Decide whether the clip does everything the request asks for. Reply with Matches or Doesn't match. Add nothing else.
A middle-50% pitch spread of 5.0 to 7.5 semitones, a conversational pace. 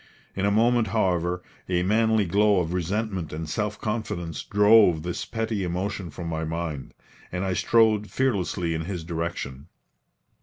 Doesn't match